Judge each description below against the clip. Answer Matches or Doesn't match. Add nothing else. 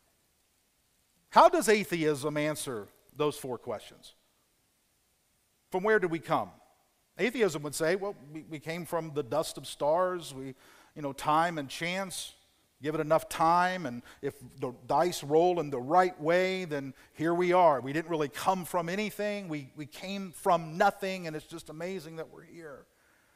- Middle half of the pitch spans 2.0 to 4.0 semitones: Matches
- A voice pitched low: Doesn't match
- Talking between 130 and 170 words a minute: Matches